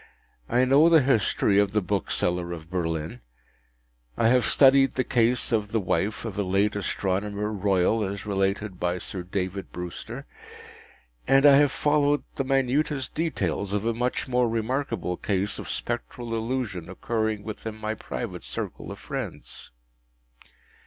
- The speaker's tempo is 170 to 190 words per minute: No, average, 145 wpm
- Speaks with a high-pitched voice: No, low, 105 Hz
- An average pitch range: Yes, average, 4.8 semitones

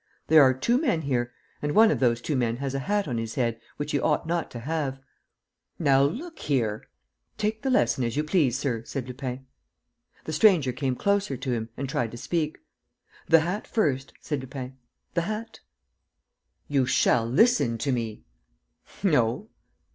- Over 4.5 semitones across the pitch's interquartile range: Yes, wide, 5.4 semitones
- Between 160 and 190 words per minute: Yes, average, 180 wpm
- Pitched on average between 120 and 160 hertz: Yes, low, 135 Hz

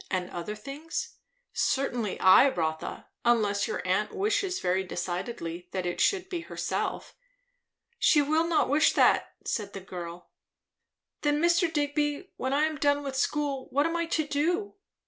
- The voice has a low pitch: No, very high, 280 Hz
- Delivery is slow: No, average, 155 wpm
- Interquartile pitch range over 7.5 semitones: Yes, wide, 8.6 semitones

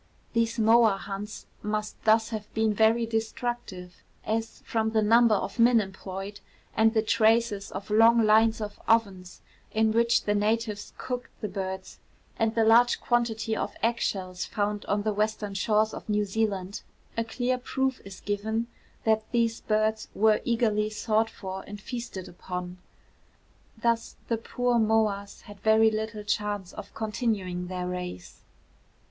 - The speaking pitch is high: Yes, high, 220 Hz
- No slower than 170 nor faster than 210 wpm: No, average, 150 wpm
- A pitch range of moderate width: No, narrow, 1.9 semitones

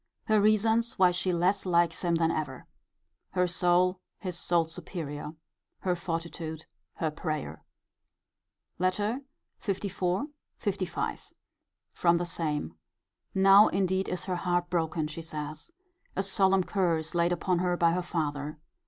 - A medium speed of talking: No, slow, 130 wpm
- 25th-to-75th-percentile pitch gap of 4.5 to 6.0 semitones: No, narrow, 2.5 semitones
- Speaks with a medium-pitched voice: Yes, medium, 175 Hz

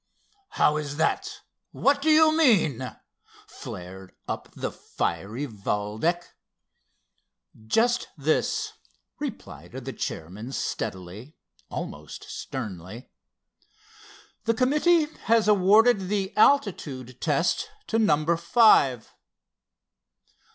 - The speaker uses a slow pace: Yes, slow, 90 wpm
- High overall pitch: No, medium, 160 Hz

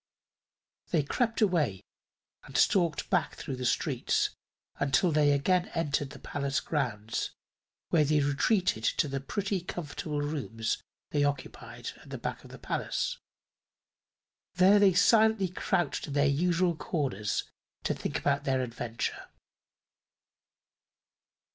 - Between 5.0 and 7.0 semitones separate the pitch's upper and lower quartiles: No, average, 4.6 semitones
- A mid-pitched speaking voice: Yes, medium, 150 Hz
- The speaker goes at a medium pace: No, slow, 125 wpm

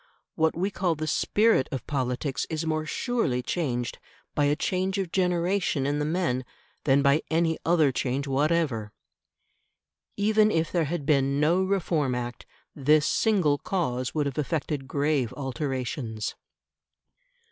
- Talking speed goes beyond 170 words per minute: No, average, 140 wpm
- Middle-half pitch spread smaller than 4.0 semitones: No, average, 4.4 semitones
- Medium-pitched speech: Yes, medium, 150 Hz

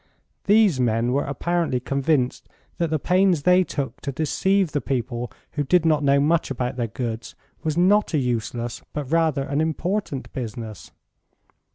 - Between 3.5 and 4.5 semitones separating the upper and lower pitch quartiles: No, average, 5.2 semitones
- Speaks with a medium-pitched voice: Yes, medium, 145 Hz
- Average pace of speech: Yes, average, 160 wpm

